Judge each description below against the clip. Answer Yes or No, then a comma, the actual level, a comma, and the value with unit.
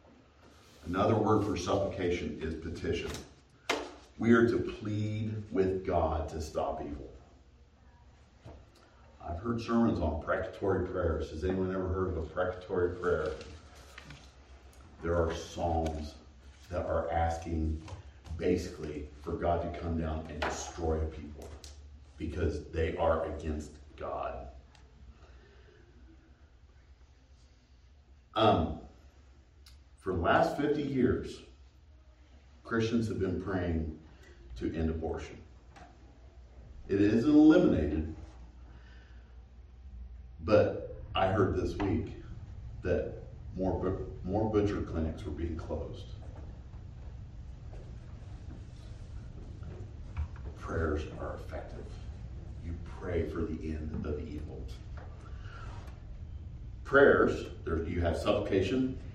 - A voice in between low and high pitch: No, very low, 80 Hz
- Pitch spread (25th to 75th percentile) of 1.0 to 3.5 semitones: No, average, 4.1 semitones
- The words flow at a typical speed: No, slow, 95 wpm